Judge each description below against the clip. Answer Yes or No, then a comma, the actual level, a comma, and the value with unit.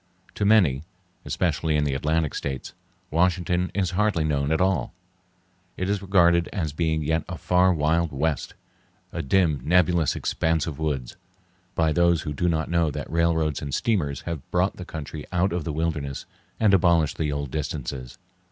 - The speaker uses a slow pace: No, average, 160 wpm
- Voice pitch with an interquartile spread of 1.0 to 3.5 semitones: Yes, average, 3.0 semitones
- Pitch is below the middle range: Yes, very low, 80 Hz